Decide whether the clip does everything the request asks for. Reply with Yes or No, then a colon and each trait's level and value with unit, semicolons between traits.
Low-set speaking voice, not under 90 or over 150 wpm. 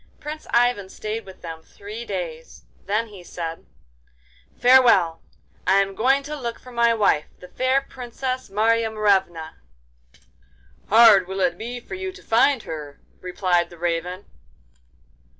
No: high, 210 Hz; average, 140 wpm